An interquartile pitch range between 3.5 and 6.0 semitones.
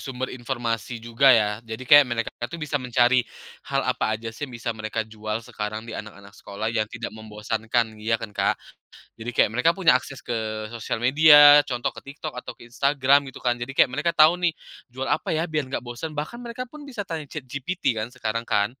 Yes: average, 4.5 semitones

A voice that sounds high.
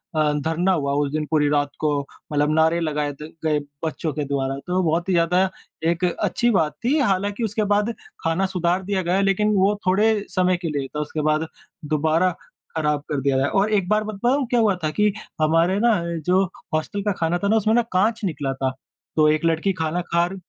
No: medium, 170 Hz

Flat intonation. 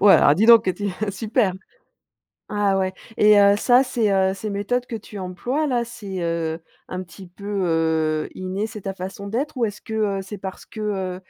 No: average, 3.0 semitones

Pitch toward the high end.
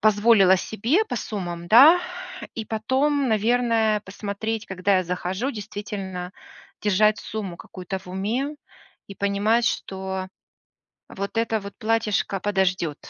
Yes: high, 205 Hz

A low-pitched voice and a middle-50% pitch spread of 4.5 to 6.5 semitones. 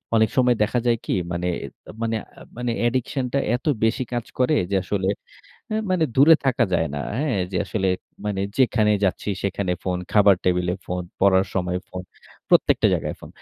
Yes: low, 105 Hz; average, 4.8 semitones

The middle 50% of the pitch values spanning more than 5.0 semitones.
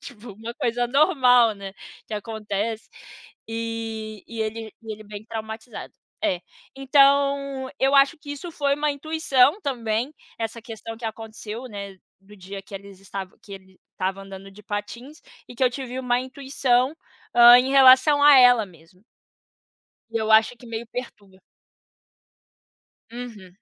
No: average, 4.0 semitones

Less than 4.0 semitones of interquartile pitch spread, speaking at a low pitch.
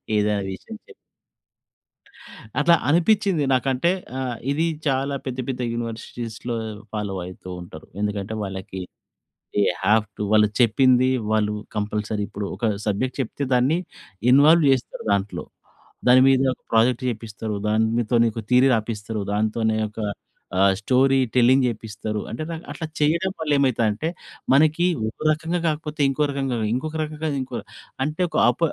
No: average, 4.8 semitones; low, 125 Hz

